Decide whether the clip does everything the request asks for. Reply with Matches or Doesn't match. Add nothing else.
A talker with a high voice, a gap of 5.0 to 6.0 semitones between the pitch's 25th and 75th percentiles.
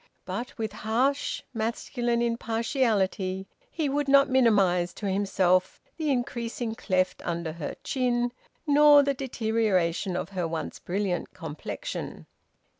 Matches